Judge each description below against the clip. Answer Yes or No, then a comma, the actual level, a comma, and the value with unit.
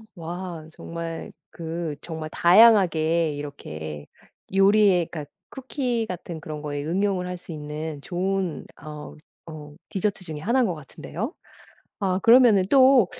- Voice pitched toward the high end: No, medium, 170 Hz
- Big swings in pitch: No, average, 4.2 semitones